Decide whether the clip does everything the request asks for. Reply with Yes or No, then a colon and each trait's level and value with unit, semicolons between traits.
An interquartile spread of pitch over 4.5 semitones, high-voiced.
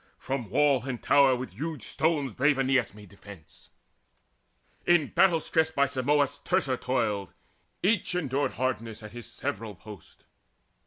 No: average, 5.1 semitones; low, 130 Hz